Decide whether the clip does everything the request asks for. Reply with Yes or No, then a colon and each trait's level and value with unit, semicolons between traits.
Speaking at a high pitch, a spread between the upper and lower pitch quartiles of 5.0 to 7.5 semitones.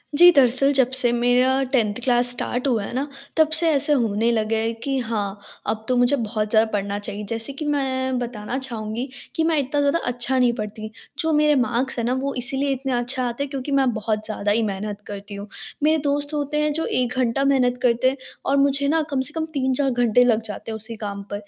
No: very high, 250 Hz; average, 3.8 semitones